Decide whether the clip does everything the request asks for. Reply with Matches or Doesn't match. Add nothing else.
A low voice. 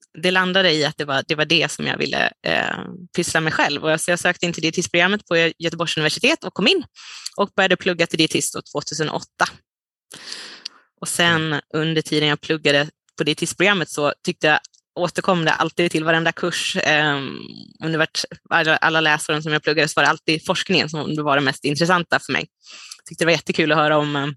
Doesn't match